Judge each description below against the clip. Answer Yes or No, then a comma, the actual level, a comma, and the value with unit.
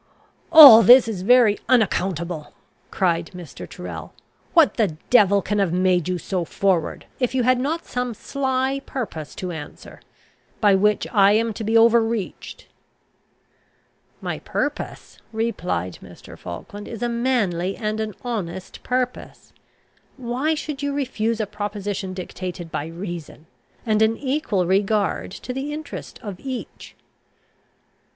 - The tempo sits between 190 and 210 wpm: No, slow, 135 wpm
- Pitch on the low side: No, high, 215 Hz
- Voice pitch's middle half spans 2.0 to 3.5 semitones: No, average, 5.2 semitones